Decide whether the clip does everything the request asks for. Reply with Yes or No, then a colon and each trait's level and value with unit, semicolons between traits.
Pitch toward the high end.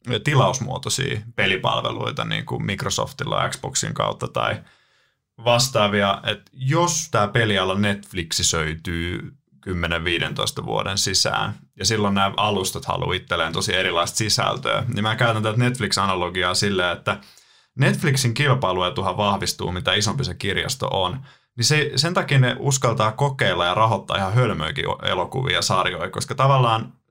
No: low, 110 Hz